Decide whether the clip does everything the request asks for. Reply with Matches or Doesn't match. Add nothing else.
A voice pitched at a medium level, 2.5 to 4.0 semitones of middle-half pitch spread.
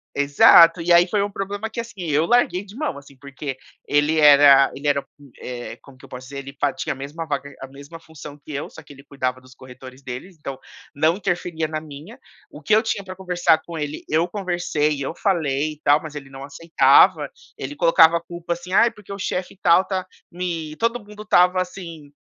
Doesn't match